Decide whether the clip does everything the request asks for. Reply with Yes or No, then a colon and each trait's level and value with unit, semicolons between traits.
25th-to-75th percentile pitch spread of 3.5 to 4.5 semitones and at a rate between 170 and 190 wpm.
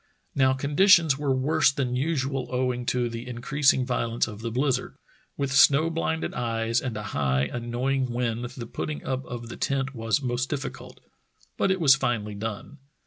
No: average, 2.8 semitones; average, 175 wpm